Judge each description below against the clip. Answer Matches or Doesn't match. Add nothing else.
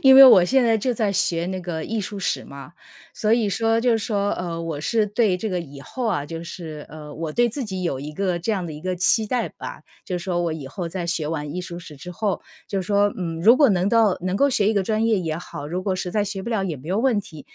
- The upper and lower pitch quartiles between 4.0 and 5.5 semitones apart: Matches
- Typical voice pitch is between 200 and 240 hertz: Doesn't match